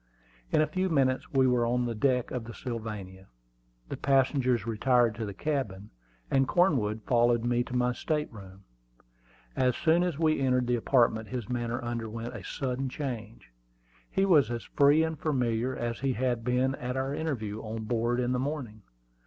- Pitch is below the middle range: Yes, low, 125 Hz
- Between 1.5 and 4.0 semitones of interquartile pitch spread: Yes, average, 2.9 semitones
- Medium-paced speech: Yes, average, 175 wpm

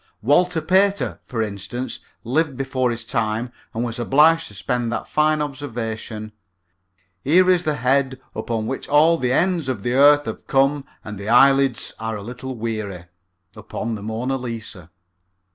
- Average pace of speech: Yes, average, 160 wpm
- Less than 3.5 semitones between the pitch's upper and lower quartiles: No, average, 4.6 semitones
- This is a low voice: Yes, low, 125 Hz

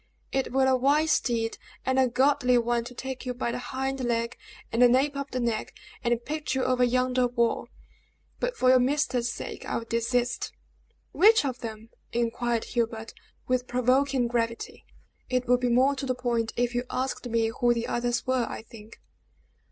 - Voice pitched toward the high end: Yes, high, 245 Hz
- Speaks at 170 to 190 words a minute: Yes, average, 185 wpm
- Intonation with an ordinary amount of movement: No, narrow, 1.7 semitones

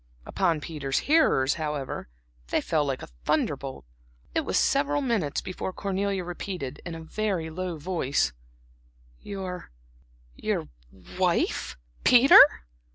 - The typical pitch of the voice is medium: Yes, medium, 170 Hz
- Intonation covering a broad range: No, average, 4.8 semitones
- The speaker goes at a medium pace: No, slow, 115 wpm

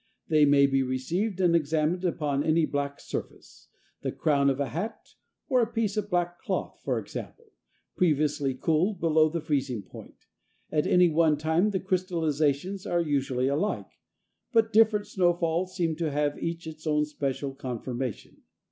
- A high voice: No, medium, 160 Hz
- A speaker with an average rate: Yes, average, 160 wpm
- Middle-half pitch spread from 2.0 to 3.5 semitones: No, average, 4.1 semitones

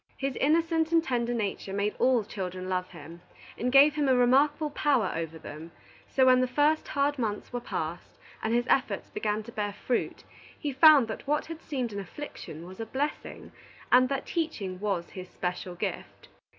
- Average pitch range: No, wide, 6.7 semitones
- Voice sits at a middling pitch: No, high, 245 Hz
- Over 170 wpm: Yes, average, 185 wpm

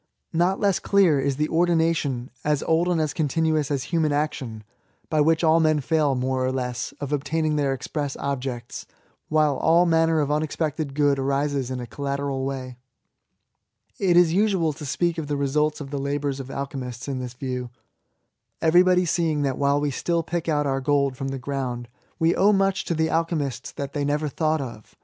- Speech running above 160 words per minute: Yes, average, 185 wpm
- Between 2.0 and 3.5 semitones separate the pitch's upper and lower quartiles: Yes, average, 3.1 semitones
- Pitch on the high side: No, medium, 145 Hz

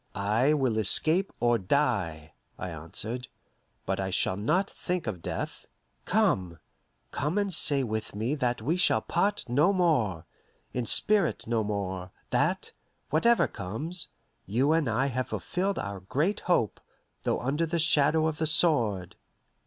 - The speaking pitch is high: No, low, 130 Hz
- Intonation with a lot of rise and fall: Yes, wide, 7.9 semitones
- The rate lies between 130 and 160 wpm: Yes, average, 145 wpm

